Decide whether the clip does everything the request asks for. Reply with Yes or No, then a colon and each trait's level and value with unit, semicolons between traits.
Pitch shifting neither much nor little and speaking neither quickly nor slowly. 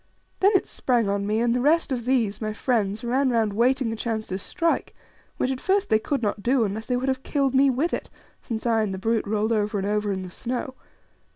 No: average, 3.7 semitones; fast, 245 wpm